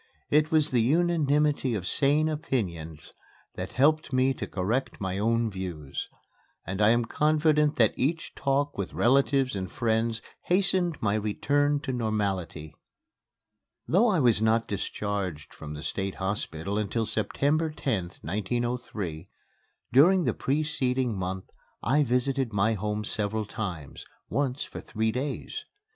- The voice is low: Yes, low, 115 Hz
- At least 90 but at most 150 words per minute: Yes, slow, 135 wpm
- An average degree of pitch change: No, wide, 6.1 semitones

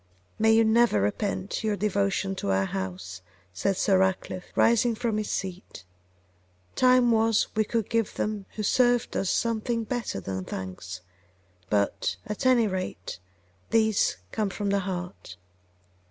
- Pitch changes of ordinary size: Yes, average, 4.3 semitones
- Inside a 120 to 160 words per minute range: Yes, average, 140 wpm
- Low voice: No, high, 200 Hz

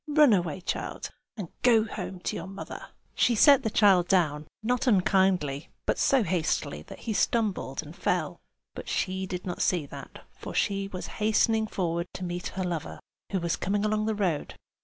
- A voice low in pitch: No, high, 190 Hz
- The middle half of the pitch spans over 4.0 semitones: No, average, 3.6 semitones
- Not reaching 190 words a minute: Yes, average, 180 wpm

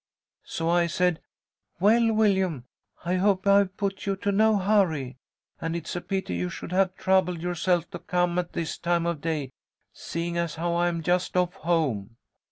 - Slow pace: No, average, 175 wpm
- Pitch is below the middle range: No, medium, 175 Hz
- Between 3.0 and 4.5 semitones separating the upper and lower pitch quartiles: No, narrow, 2.4 semitones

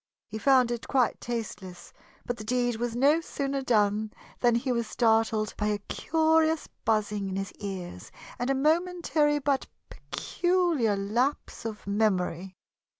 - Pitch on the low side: No, high, 235 Hz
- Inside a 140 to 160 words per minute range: Yes, average, 145 wpm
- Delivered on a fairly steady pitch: No, average, 4.8 semitones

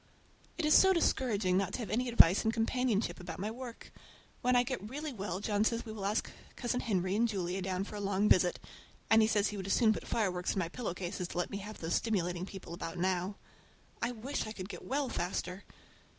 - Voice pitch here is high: Yes, high, 205 Hz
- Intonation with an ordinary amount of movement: Yes, average, 4.1 semitones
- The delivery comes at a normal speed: No, fast, 235 wpm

